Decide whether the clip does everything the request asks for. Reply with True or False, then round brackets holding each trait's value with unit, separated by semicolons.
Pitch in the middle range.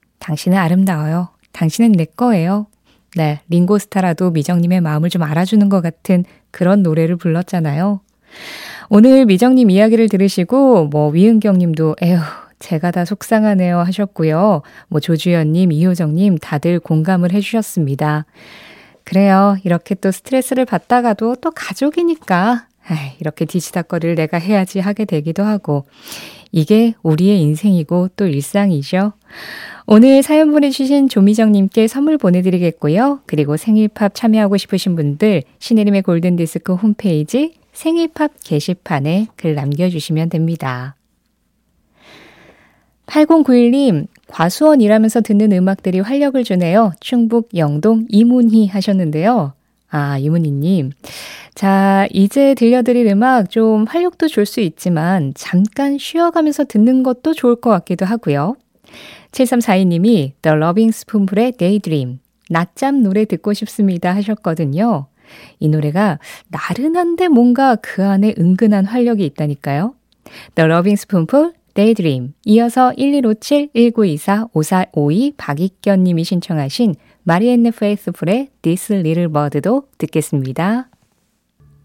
False (195 Hz)